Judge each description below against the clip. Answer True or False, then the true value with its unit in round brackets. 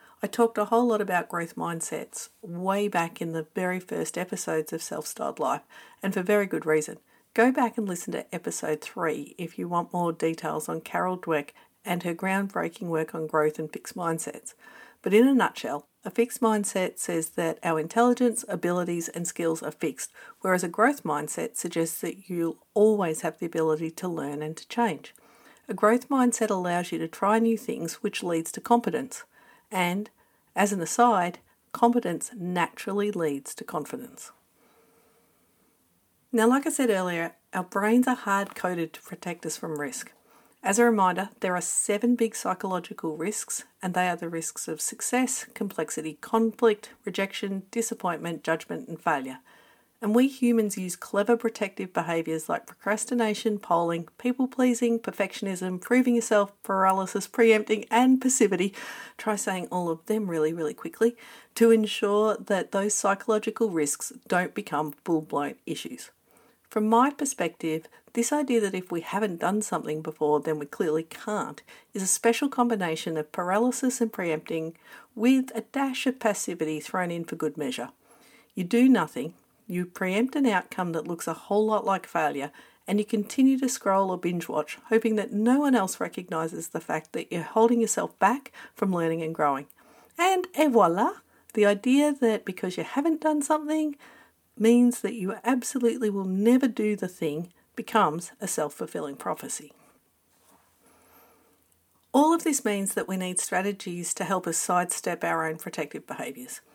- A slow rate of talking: False (165 wpm)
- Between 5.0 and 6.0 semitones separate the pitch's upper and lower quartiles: True (5.3 semitones)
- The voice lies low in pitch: False (200 Hz)